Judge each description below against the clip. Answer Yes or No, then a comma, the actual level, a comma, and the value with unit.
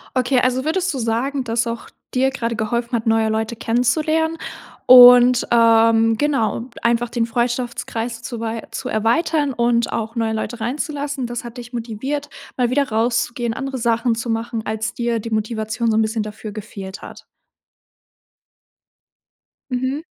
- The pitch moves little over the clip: Yes, narrow, 2.0 semitones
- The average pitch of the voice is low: No, high, 235 Hz